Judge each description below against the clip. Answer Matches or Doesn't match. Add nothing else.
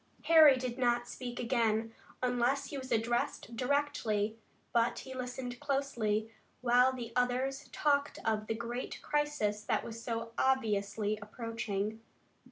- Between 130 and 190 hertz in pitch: Doesn't match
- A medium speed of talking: Doesn't match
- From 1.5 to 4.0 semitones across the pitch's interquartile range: Matches